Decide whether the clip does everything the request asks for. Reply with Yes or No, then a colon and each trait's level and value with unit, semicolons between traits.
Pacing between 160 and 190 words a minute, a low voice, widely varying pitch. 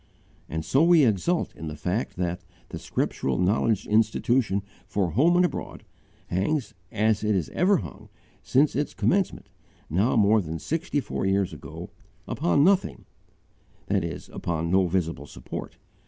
No: average, 150 wpm; low, 105 Hz; wide, 8.0 semitones